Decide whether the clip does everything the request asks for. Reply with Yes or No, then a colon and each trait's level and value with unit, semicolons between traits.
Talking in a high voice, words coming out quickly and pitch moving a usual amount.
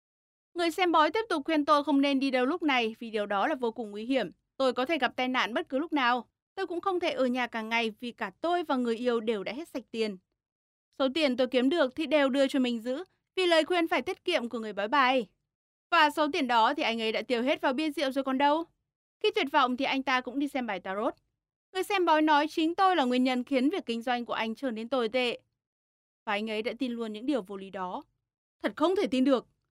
Yes: very high, 265 Hz; fast, 270 wpm; average, 4.8 semitones